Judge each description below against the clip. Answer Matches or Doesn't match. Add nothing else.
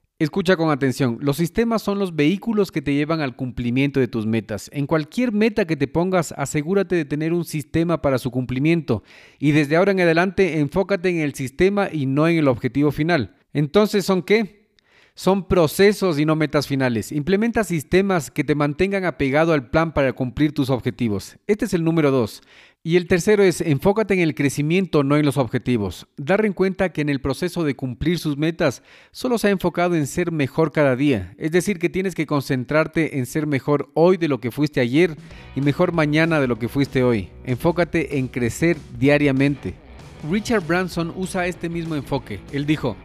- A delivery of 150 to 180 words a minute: Doesn't match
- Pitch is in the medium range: Matches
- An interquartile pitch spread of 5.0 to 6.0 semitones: Doesn't match